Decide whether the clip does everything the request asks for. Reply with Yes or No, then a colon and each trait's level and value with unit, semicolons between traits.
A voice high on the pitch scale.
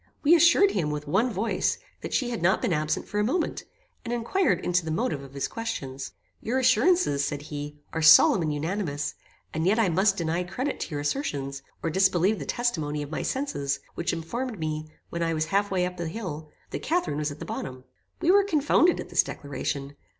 No: medium, 170 Hz